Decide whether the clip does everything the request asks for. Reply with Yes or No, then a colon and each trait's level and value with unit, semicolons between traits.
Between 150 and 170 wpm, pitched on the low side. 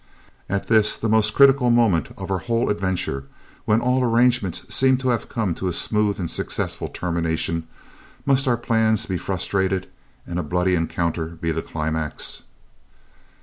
Yes: average, 155 wpm; low, 100 Hz